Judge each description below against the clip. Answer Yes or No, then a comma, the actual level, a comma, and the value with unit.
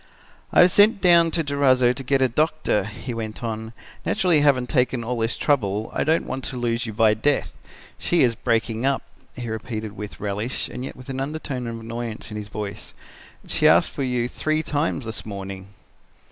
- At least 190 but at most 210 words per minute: Yes, average, 195 wpm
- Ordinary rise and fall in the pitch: Yes, average, 4.2 semitones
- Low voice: Yes, low, 125 Hz